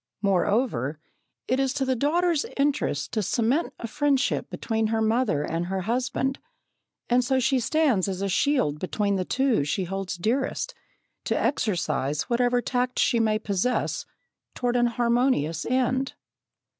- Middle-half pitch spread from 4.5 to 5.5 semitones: Yes, average, 5.2 semitones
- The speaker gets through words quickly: No, average, 145 wpm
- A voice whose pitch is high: Yes, high, 235 Hz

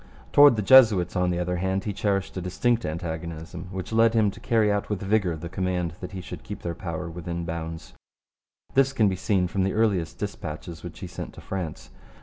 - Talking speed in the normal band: No, fast, 210 wpm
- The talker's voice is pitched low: Yes, very low, 95 Hz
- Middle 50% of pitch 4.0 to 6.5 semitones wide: No, average, 3.4 semitones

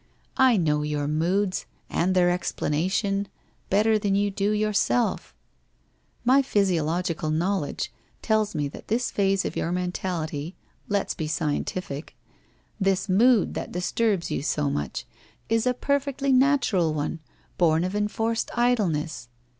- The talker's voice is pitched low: No, high, 190 Hz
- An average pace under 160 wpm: Yes, average, 140 wpm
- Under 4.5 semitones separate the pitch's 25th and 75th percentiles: No, average, 5.1 semitones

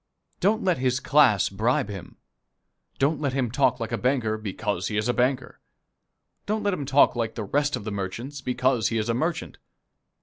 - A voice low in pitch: Yes, low, 125 Hz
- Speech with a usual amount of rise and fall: Yes, average, 4.5 semitones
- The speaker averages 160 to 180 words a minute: No, average, 195 wpm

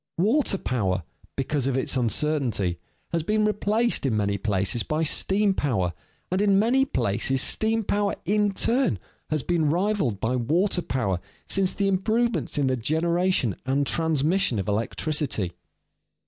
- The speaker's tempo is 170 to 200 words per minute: No, average, 145 wpm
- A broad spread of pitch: Yes, wide, 8.6 semitones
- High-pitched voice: No, medium, 155 Hz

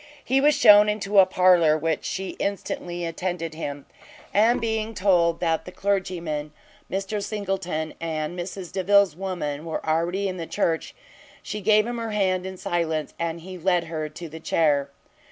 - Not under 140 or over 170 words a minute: Yes, average, 165 wpm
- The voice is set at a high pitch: No, medium, 180 Hz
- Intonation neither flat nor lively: Yes, average, 3.5 semitones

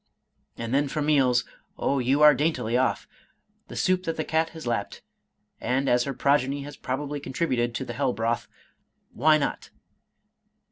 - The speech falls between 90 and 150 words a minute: No, average, 180 wpm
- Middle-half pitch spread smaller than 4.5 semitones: Yes, average, 3.4 semitones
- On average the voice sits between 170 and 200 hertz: No, medium, 140 Hz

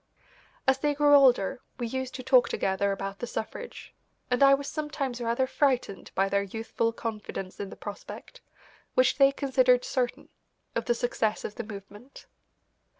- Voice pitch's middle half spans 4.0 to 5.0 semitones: Yes, average, 4.4 semitones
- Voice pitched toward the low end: No, high, 245 Hz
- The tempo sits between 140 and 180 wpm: Yes, average, 160 wpm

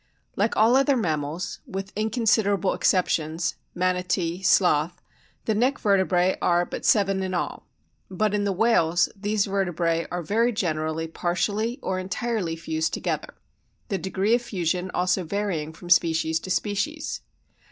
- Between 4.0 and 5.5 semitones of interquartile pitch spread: No, average, 3.3 semitones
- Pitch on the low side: No, medium, 185 Hz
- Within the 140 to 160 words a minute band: Yes, average, 150 wpm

